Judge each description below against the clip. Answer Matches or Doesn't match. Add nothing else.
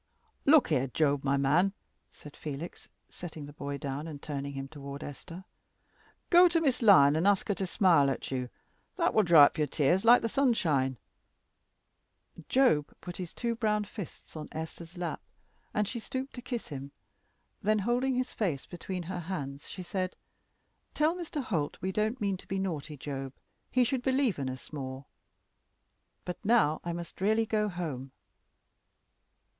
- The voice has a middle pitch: Matches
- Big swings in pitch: Matches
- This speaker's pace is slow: Doesn't match